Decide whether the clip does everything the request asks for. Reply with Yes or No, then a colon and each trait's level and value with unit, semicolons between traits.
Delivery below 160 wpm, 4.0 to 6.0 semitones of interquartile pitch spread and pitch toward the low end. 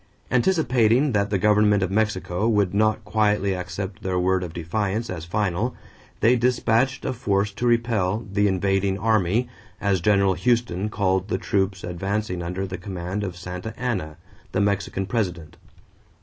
No: average, 150 wpm; average, 2.9 semitones; low, 100 Hz